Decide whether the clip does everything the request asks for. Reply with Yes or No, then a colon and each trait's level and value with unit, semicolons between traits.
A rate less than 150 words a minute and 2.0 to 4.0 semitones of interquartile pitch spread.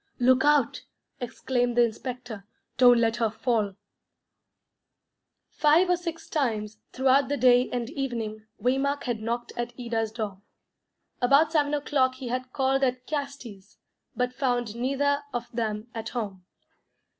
Yes: average, 140 wpm; average, 3.1 semitones